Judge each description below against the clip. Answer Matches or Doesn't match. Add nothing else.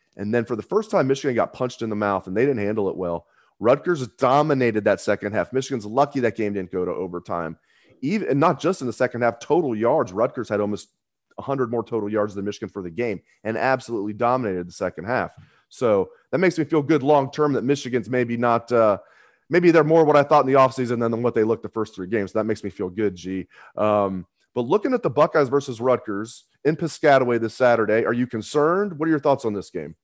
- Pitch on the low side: Matches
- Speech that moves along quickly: Matches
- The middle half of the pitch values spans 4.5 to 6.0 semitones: Matches